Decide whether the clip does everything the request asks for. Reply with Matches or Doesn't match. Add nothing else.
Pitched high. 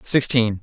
Doesn't match